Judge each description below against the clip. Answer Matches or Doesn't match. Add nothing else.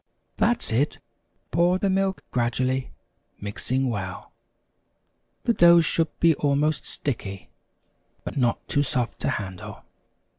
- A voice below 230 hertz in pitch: Matches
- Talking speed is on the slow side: Matches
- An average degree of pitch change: Doesn't match